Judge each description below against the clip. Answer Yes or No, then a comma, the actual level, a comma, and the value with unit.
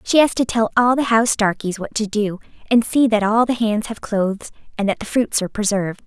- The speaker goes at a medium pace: No, fast, 245 wpm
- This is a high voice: Yes, high, 220 Hz